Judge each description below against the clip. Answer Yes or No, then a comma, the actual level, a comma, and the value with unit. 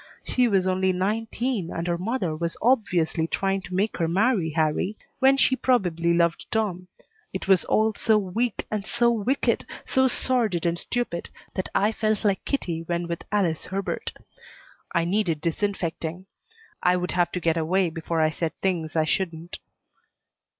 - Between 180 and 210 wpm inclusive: No, average, 165 wpm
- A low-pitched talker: No, medium, 185 Hz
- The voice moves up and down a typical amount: Yes, average, 4.2 semitones